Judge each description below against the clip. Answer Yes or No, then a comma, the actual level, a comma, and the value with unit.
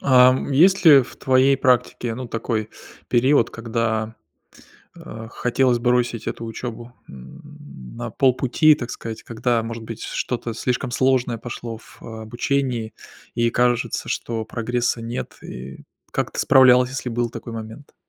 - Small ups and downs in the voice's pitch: Yes, narrow, 2.1 semitones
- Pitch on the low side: Yes, low, 120 Hz